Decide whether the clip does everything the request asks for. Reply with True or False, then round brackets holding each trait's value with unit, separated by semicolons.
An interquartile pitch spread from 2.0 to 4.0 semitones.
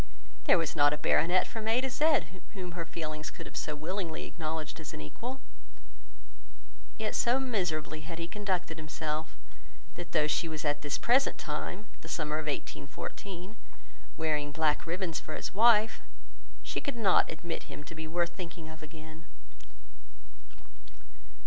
True (3.7 semitones)